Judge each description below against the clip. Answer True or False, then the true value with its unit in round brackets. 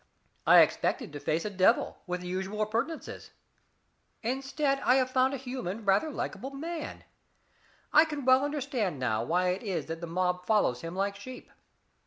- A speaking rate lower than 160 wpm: False (170 wpm)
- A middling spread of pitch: False (6.9 semitones)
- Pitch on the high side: True (210 Hz)